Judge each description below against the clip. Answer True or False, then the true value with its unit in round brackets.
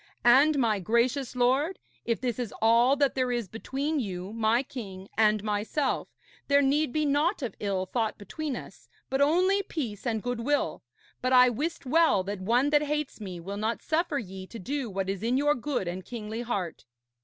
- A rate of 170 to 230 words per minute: True (190 wpm)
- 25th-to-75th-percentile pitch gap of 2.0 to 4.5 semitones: False (5.2 semitones)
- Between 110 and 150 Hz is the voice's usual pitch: False (245 Hz)